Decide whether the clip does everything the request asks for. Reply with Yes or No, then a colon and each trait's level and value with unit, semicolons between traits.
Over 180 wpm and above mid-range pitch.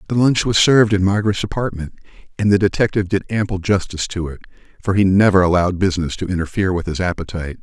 No: average, 195 wpm; very low, 95 Hz